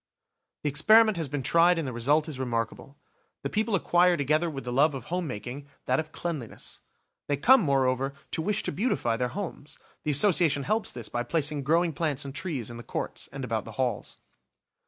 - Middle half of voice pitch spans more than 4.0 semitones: Yes, average, 4.5 semitones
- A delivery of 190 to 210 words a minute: Yes, average, 195 wpm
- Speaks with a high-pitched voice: No, medium, 150 Hz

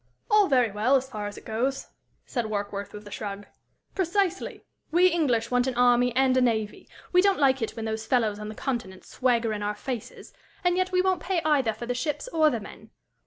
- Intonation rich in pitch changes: Yes, wide, 5.8 semitones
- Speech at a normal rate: No, fast, 215 wpm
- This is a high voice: Yes, high, 245 Hz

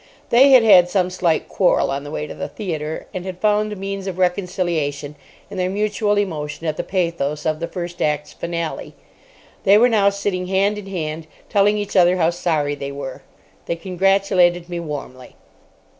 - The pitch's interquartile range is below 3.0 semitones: No, average, 4.0 semitones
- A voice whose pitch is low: No, medium, 180 Hz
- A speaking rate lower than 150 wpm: No, average, 185 wpm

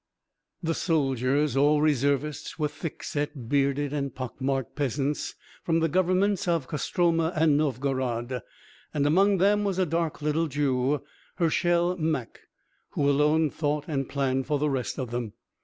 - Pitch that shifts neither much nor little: Yes, average, 3.3 semitones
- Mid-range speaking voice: Yes, medium, 150 Hz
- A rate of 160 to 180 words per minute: No, average, 150 wpm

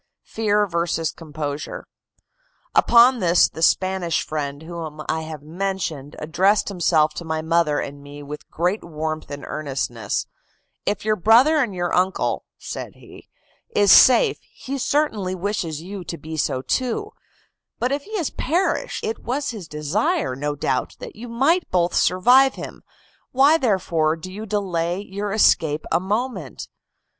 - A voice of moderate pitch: Yes, medium, 180 Hz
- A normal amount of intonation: No, wide, 6.1 semitones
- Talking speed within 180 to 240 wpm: No, average, 150 wpm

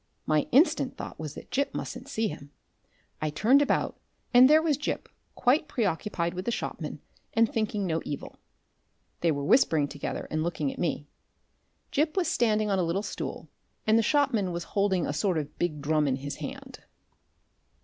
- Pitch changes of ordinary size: No, wide, 7.8 semitones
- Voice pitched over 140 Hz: Yes, high, 190 Hz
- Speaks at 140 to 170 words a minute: No, average, 180 wpm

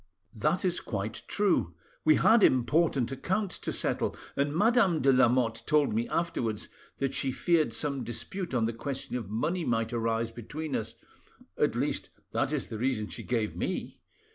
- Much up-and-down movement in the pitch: Yes, wide, 5.9 semitones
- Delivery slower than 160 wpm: No, average, 165 wpm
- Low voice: Yes, low, 130 Hz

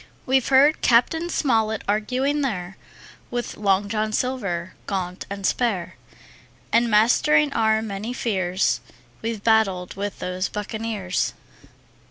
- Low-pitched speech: No, high, 215 Hz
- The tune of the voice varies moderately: Yes, average, 3.7 semitones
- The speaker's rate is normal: No, slow, 115 wpm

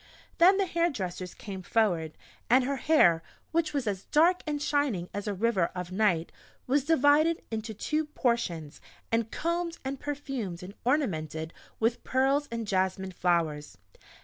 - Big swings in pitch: Yes, wide, 8.0 semitones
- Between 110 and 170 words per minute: Yes, average, 150 wpm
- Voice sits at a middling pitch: No, high, 230 Hz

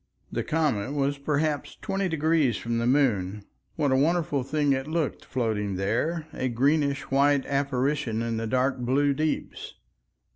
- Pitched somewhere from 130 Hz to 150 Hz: Yes, medium, 140 Hz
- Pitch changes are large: No, average, 3.8 semitones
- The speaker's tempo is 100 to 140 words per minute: No, average, 150 wpm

